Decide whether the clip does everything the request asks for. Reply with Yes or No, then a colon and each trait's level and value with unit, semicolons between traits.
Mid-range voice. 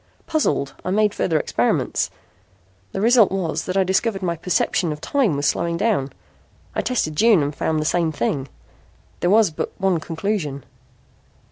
Yes: medium, 175 Hz